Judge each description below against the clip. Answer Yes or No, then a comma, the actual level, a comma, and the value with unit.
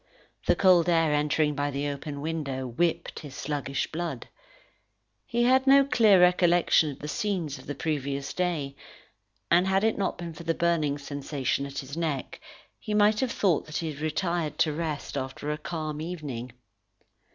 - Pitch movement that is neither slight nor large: Yes, average, 3.7 semitones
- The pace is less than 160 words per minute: No, average, 175 wpm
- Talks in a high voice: No, medium, 155 Hz